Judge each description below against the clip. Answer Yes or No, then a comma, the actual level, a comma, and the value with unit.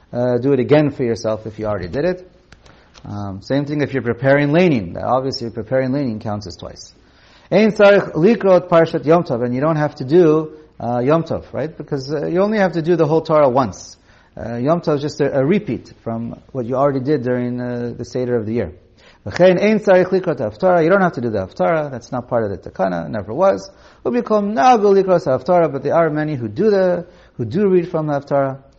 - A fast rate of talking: Yes, fast, 215 wpm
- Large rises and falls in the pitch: Yes, wide, 6.6 semitones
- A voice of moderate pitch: Yes, medium, 145 Hz